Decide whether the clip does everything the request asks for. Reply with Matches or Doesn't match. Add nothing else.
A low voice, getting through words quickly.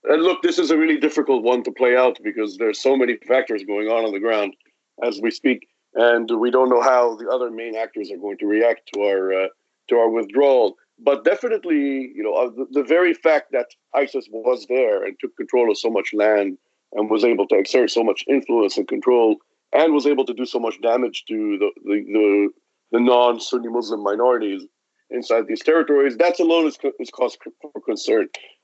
Matches